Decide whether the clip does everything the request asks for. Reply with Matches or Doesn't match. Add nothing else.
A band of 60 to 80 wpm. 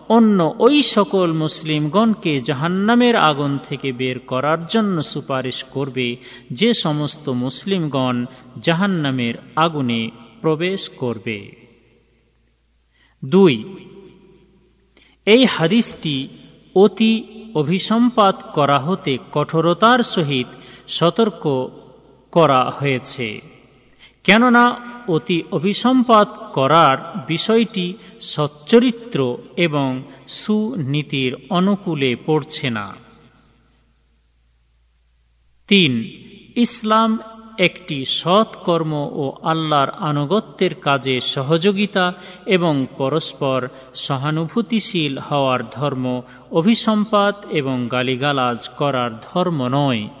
Matches